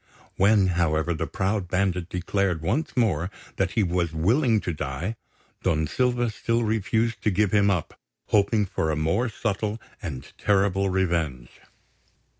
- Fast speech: No, average, 145 wpm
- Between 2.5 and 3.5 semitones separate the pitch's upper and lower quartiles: No, average, 4.2 semitones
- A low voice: Yes, very low, 95 Hz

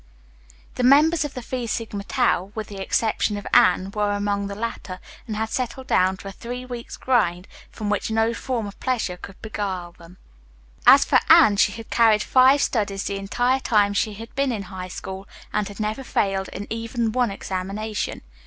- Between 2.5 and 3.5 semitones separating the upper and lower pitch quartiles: Yes, average, 3.2 semitones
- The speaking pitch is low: No, high, 210 Hz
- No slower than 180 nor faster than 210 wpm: Yes, average, 190 wpm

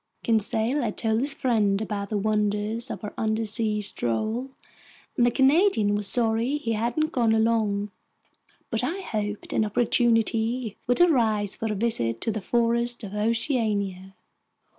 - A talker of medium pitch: No, high, 225 Hz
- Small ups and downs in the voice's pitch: Yes, narrow, 2.3 semitones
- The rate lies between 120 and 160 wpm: Yes, average, 145 wpm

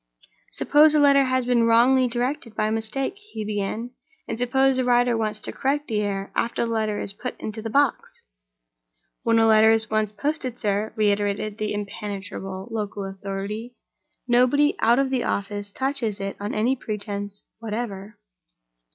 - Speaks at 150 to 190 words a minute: Yes, average, 160 wpm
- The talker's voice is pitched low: No, high, 225 Hz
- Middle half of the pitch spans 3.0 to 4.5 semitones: Yes, average, 3.3 semitones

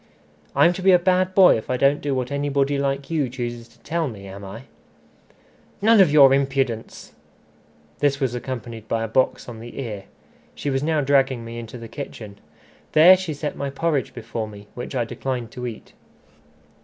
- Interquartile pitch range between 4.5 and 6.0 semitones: No, average, 3.8 semitones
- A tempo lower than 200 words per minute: Yes, average, 190 wpm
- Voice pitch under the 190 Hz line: Yes, low, 135 Hz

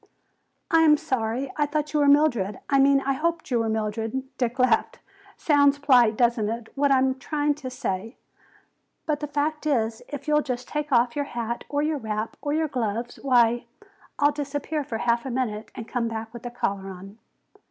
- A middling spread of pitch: Yes, average, 4.2 semitones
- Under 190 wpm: No, average, 195 wpm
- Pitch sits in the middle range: No, very high, 260 Hz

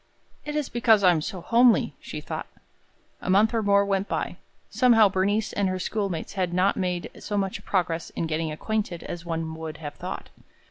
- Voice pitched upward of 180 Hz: Yes, high, 190 Hz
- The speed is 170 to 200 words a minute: Yes, average, 190 wpm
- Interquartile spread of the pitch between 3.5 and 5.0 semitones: Yes, average, 4.0 semitones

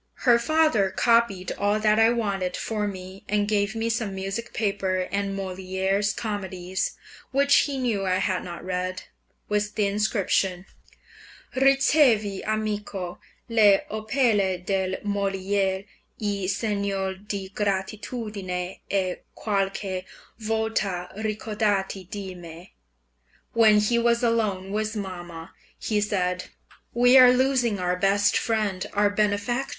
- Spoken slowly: Yes, slow, 120 wpm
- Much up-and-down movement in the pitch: No, narrow, 2.5 semitones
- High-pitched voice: Yes, high, 205 Hz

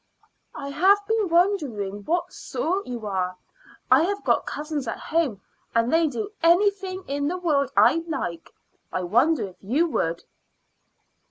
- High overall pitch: Yes, very high, 305 Hz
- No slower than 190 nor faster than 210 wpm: No, average, 150 wpm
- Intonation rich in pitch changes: Yes, wide, 7.7 semitones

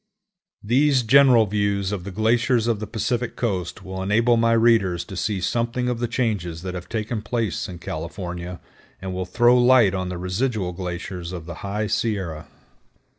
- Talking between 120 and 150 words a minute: No, average, 175 wpm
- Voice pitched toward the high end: No, low, 105 Hz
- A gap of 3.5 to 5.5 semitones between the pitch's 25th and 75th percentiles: Yes, average, 4.3 semitones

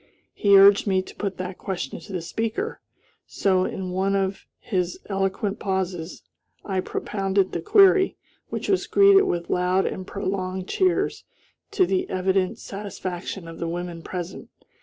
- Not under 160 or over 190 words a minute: No, average, 150 wpm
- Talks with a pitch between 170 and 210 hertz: Yes, high, 190 Hz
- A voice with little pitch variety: Yes, narrow, 1.8 semitones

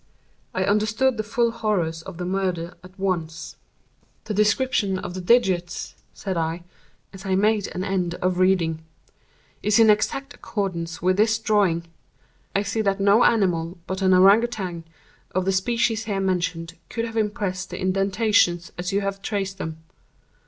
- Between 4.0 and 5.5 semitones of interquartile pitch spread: No, average, 3.0 semitones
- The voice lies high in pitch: Yes, high, 195 Hz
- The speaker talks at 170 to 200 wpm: No, average, 160 wpm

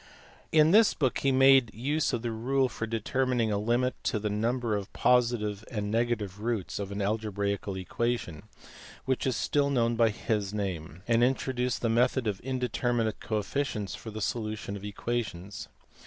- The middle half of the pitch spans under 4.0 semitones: Yes, average, 3.3 semitones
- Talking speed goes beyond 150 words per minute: Yes, average, 160 wpm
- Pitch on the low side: Yes, low, 115 Hz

